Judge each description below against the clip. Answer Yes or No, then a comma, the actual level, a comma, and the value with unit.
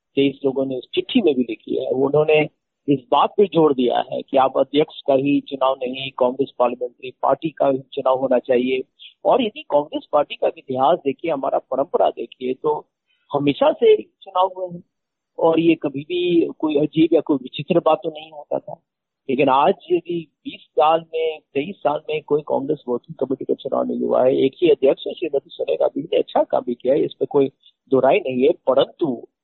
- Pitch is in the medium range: Yes, medium, 155 Hz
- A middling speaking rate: No, fast, 200 wpm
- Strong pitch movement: Yes, wide, 7.4 semitones